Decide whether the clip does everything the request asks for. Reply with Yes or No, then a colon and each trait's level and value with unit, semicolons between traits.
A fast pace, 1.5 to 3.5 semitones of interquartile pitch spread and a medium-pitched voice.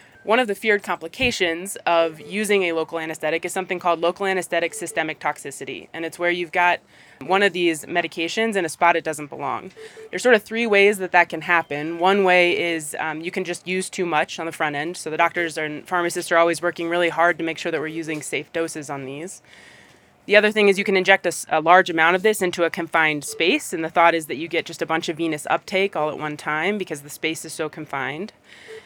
Yes: fast, 240 wpm; narrow, 2.6 semitones; medium, 170 Hz